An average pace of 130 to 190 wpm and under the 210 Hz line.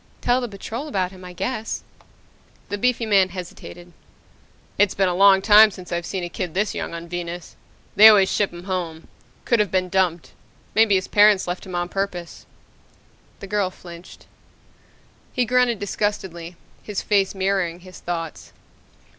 Yes: average, 165 wpm; high, 190 Hz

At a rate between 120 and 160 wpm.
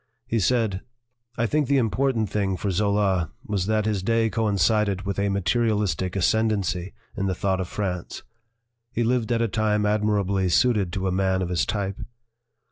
No: average, 175 wpm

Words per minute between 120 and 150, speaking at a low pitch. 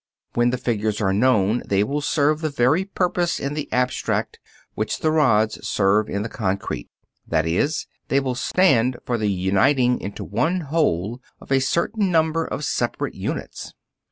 No: average, 165 wpm; low, 125 Hz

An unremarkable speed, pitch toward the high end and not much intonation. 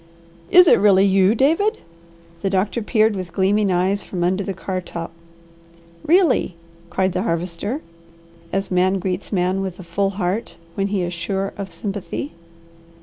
Yes: average, 155 wpm; high, 195 Hz; narrow, 2.1 semitones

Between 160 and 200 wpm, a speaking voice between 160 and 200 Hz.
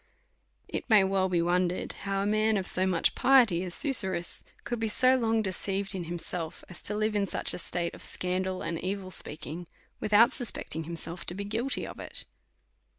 Yes: average, 195 wpm; high, 190 Hz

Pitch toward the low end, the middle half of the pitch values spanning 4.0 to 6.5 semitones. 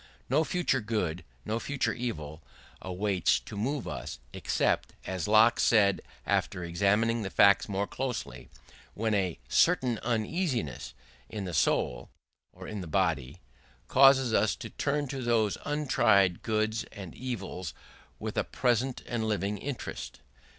Yes: low, 110 Hz; average, 4.6 semitones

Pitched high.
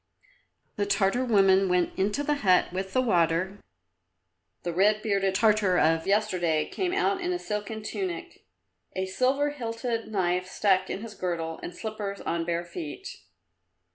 Yes: high, 200 Hz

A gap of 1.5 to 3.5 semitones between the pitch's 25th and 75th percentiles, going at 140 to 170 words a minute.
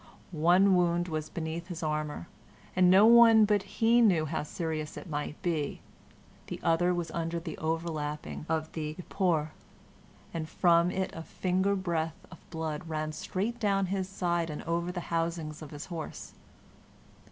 Yes: average, 2.8 semitones; average, 160 wpm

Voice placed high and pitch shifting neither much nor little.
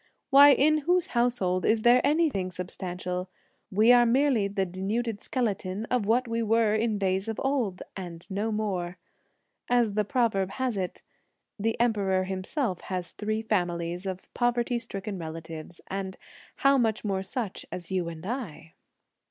Yes: high, 210 Hz; average, 4.4 semitones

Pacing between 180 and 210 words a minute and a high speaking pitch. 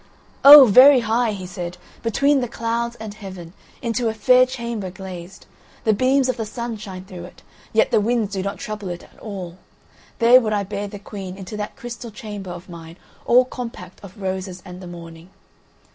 Yes: average, 190 wpm; high, 205 Hz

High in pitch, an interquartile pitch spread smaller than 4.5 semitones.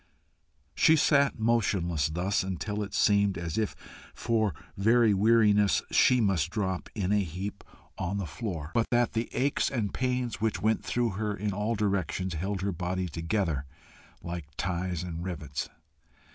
No: low, 100 Hz; average, 3.9 semitones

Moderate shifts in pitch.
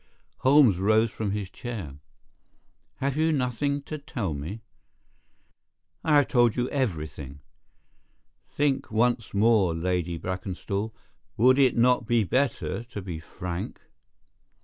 No: wide, 5.9 semitones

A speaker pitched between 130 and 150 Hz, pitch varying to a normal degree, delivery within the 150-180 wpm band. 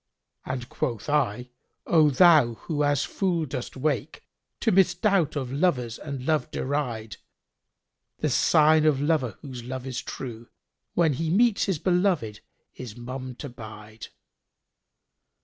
No: medium, 140 Hz; average, 4.4 semitones; average, 140 wpm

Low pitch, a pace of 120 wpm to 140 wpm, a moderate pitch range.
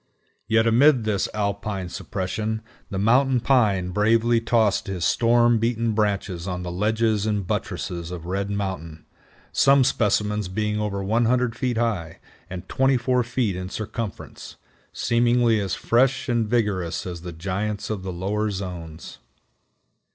Yes: low, 105 Hz; slow, 135 wpm; average, 3.6 semitones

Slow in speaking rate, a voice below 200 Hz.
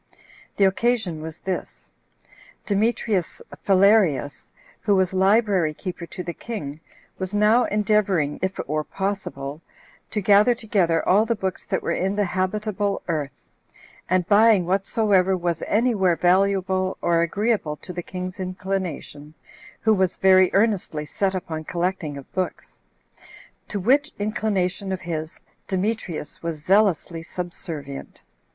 Yes: slow, 130 wpm; high, 190 Hz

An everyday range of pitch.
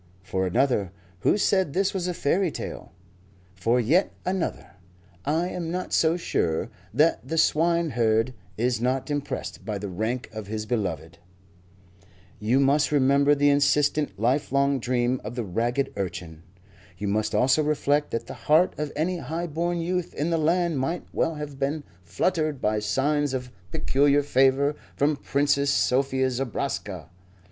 Yes: average, 5.0 semitones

